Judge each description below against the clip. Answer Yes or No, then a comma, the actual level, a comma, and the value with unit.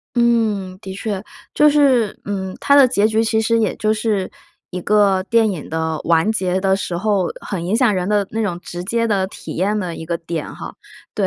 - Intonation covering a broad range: No, average, 3.2 semitones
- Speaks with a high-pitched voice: Yes, high, 200 Hz